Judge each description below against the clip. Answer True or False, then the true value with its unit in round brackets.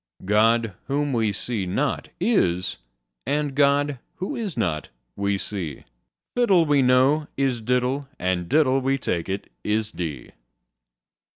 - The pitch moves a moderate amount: False (6.3 semitones)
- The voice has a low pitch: True (125 Hz)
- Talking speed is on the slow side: True (130 wpm)